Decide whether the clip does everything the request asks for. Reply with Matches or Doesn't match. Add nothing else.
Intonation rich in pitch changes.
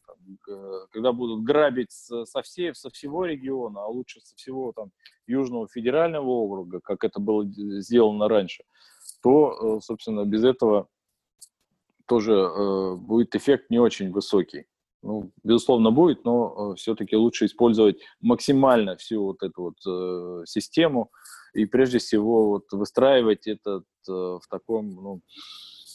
Doesn't match